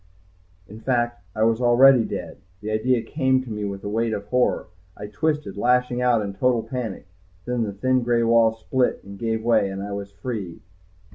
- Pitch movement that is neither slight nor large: Yes, average, 3.2 semitones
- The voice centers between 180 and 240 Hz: No, low, 115 Hz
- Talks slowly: No, average, 195 wpm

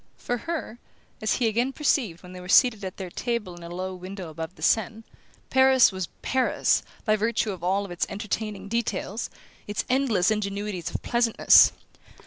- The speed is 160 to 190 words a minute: Yes, average, 170 wpm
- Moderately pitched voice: No, high, 210 Hz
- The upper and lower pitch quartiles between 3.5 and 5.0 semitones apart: Yes, average, 4.2 semitones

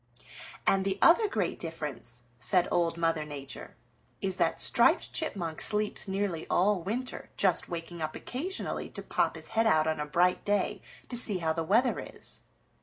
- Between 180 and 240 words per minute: No, average, 170 wpm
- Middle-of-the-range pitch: Yes, medium, 180 Hz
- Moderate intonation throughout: Yes, average, 4.3 semitones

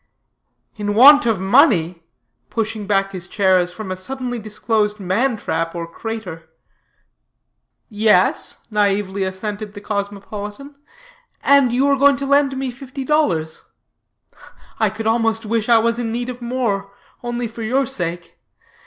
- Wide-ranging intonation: No, average, 3.8 semitones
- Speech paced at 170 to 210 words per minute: No, average, 145 wpm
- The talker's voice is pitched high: Yes, high, 220 Hz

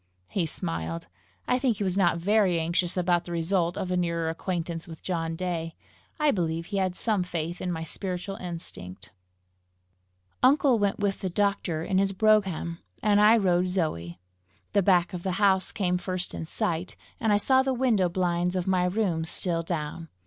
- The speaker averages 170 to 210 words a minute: Yes, average, 180 wpm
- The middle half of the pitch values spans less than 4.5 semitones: Yes, average, 2.9 semitones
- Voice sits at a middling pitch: Yes, medium, 180 Hz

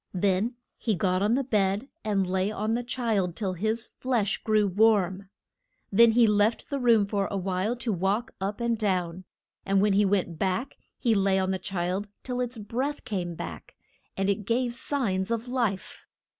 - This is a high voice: Yes, high, 205 Hz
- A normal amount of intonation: Yes, average, 3.4 semitones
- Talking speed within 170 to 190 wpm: Yes, average, 185 wpm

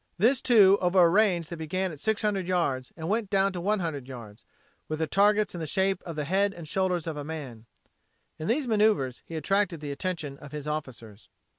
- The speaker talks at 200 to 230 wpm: Yes, fast, 205 wpm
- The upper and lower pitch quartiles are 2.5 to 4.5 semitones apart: No, average, 4.9 semitones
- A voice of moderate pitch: Yes, medium, 170 Hz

